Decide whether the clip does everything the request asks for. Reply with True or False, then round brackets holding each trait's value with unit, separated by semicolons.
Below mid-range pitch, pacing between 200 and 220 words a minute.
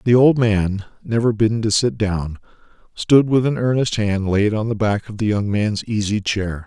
True (110 Hz; 205 wpm)